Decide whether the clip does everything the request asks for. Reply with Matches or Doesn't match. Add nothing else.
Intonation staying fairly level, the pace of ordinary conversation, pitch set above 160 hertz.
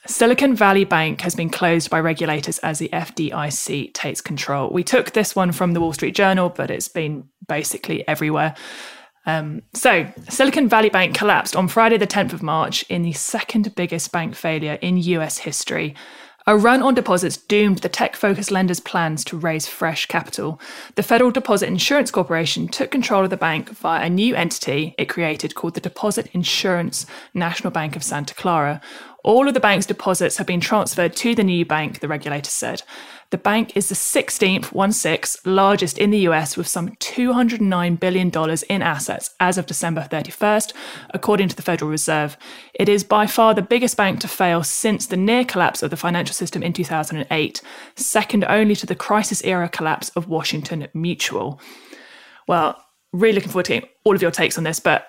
Doesn't match